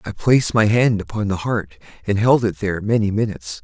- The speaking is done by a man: Yes, male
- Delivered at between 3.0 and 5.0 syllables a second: No, 5.8 syllables/s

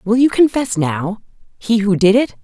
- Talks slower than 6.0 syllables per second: Yes, 4.7 syllables/s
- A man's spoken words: No, female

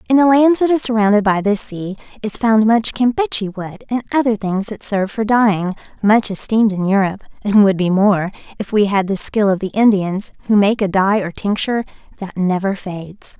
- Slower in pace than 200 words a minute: No, fast, 205 wpm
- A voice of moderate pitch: No, high, 210 Hz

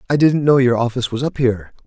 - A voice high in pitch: No, low, 130 Hz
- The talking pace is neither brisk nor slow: No, fast, 260 wpm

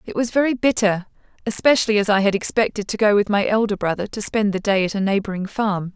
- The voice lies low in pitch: No, high, 205 Hz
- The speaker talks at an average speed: No, fast, 230 wpm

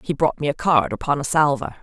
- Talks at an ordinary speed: No, fast, 265 wpm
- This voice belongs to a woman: Yes, female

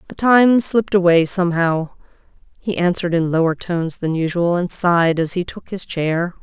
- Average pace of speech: Yes, average, 175 wpm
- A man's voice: No, female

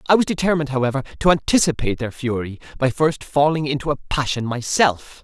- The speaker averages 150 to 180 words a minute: Yes, average, 170 wpm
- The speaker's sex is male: Yes, male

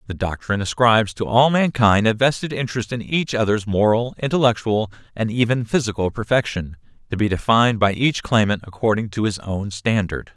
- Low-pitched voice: Yes, low, 110 Hz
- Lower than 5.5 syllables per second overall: No, 5.6 syllables/s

